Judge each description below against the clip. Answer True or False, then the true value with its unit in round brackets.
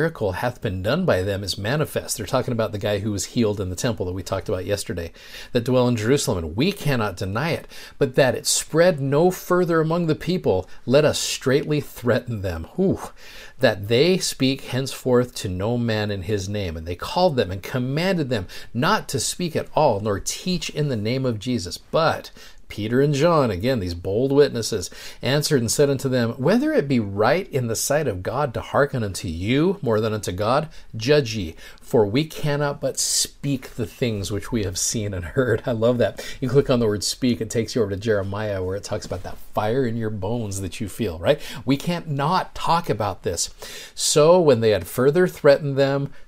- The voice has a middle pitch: False (120 Hz)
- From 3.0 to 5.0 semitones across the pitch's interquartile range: False (5.5 semitones)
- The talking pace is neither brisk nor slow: False (210 wpm)